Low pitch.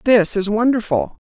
No: high, 215 Hz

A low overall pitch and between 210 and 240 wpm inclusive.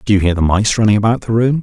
No: low, 110 Hz; fast, 330 wpm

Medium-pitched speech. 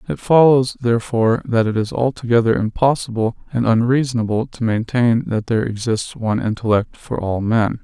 No: low, 115 Hz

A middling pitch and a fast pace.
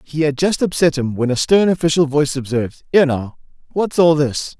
Yes: medium, 150 Hz; fast, 210 wpm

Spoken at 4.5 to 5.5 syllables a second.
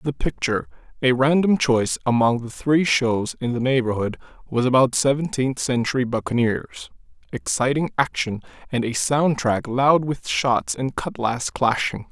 Yes: 4.6 syllables/s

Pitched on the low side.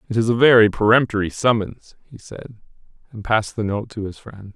Yes: low, 110 Hz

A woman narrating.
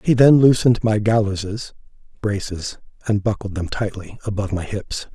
No: male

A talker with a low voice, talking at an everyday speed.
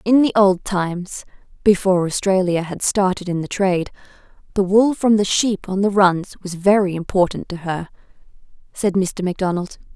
No: high, 190 Hz; average, 165 wpm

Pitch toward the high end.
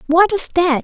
Yes: very high, 340 Hz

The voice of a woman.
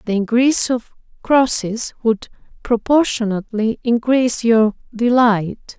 Yes: female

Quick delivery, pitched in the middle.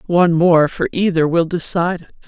No: average, 185 wpm; medium, 170 Hz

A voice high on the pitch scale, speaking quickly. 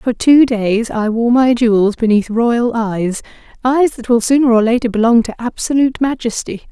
No: high, 235 Hz; average, 170 wpm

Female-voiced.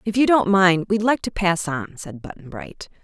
Yes: female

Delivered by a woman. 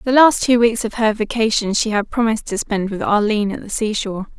Yes: female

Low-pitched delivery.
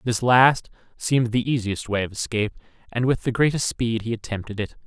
Yes: low, 115 Hz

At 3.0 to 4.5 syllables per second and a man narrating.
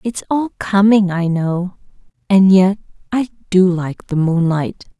No: 3.9 syllables/s; female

